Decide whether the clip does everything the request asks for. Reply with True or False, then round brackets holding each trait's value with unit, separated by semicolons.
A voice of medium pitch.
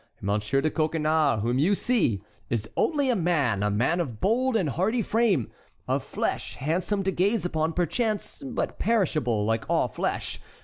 True (160 Hz)